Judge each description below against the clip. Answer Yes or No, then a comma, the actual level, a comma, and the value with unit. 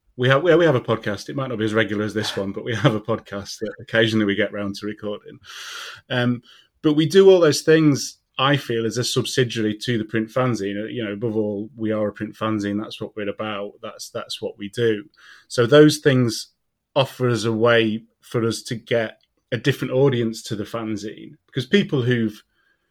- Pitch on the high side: No, low, 115 Hz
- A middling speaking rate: No, fast, 210 wpm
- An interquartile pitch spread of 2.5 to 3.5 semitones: Yes, average, 3.2 semitones